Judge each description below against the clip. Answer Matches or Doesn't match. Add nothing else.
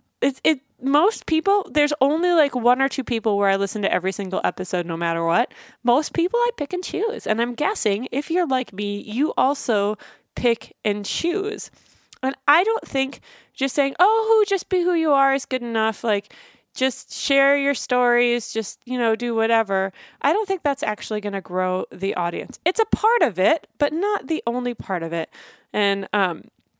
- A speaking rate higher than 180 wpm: Matches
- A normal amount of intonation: Doesn't match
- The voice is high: Matches